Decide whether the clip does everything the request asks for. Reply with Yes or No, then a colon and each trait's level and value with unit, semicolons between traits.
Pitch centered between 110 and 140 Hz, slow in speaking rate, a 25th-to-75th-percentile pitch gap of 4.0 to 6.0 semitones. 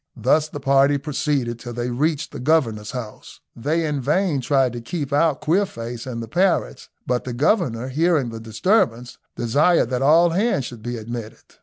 No: low, 135 Hz; average, 175 wpm; average, 4.6 semitones